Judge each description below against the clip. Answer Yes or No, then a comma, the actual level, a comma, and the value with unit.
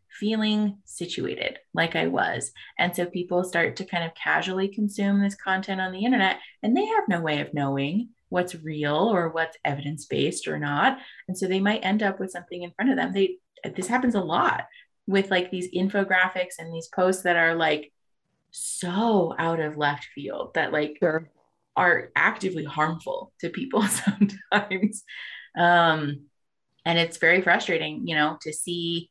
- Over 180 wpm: No, average, 170 wpm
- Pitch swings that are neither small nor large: Yes, average, 3.4 semitones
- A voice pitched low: No, medium, 180 Hz